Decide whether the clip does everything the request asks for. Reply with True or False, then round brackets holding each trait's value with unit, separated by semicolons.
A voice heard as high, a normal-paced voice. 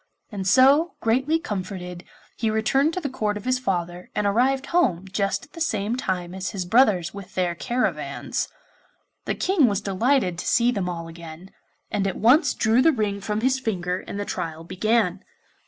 True (205 Hz; 185 wpm)